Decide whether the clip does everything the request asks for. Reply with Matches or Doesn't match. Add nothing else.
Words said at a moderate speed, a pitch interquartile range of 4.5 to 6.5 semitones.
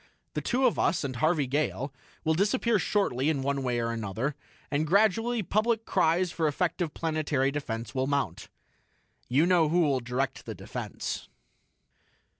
Matches